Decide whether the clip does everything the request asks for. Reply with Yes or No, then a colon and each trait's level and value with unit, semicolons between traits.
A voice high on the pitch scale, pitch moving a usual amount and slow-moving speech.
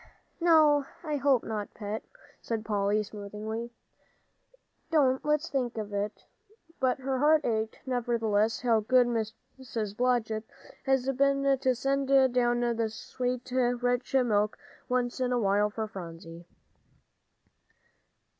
Yes: high, 240 Hz; average, 3.3 semitones; slow, 120 wpm